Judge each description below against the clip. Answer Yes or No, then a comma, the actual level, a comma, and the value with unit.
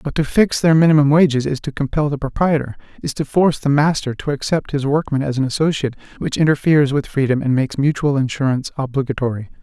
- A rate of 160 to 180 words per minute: No, average, 200 wpm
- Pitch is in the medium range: Yes, medium, 145 Hz